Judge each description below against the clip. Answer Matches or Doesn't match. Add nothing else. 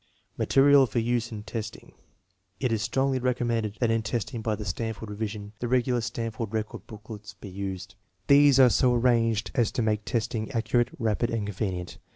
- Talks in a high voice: Doesn't match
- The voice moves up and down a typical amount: Doesn't match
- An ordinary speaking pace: Matches